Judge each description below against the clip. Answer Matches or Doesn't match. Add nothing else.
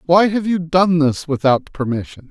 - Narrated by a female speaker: Doesn't match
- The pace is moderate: Matches